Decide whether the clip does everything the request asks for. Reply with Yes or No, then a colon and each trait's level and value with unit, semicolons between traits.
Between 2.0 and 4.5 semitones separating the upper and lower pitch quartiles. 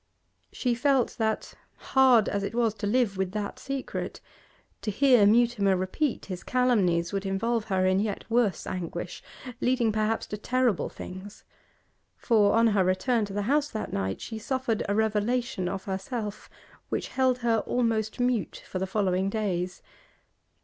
Yes: average, 3.9 semitones